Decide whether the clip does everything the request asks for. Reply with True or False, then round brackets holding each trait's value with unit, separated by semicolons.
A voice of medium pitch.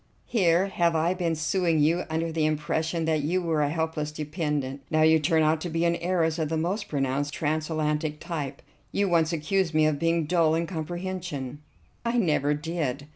True (160 Hz)